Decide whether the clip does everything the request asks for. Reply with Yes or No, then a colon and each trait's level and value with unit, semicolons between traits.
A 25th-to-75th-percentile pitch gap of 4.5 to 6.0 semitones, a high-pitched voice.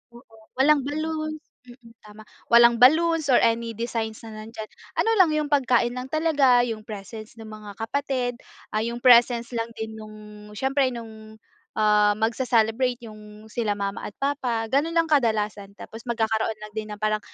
No: average, 3.5 semitones; high, 230 Hz